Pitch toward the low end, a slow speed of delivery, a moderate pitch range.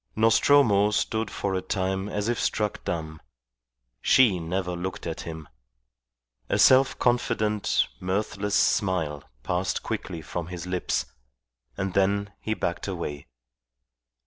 Yes: very low, 95 Hz; slow, 120 wpm; average, 3.2 semitones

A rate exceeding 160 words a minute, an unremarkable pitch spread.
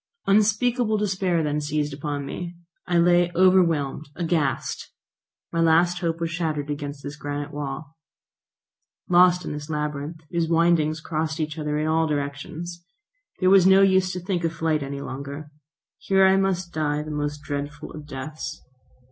No: average, 155 wpm; average, 3.1 semitones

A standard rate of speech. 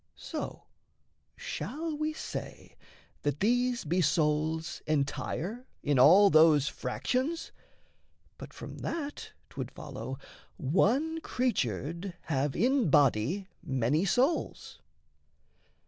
No: slow, 95 wpm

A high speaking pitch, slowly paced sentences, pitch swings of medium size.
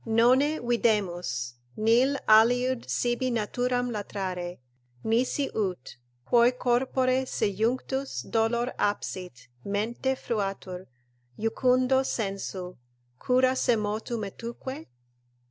Yes: high, 230 Hz; slow, 80 wpm; average, 3.8 semitones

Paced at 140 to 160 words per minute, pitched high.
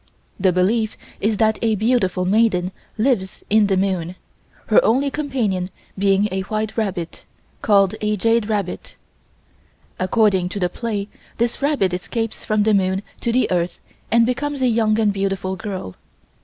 Yes: average, 155 wpm; high, 210 Hz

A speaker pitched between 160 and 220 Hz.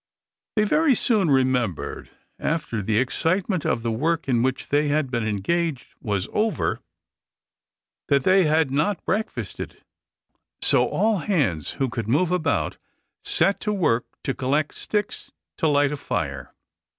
No: medium, 145 Hz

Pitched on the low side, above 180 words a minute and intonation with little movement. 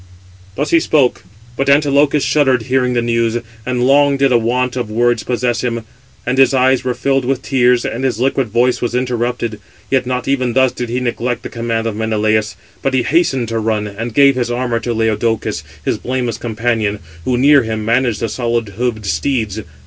Yes: low, 120 Hz; average, 195 wpm; narrow, 2.3 semitones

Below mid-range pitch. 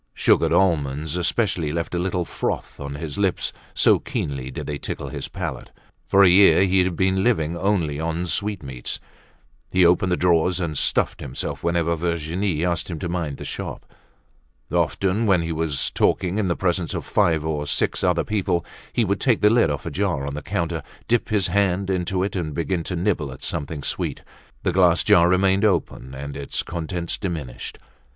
Yes: very low, 85 Hz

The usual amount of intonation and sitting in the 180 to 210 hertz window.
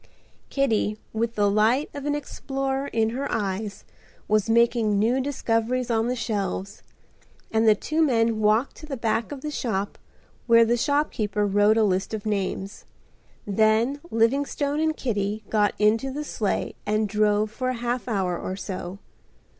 No: average, 3.5 semitones; high, 225 Hz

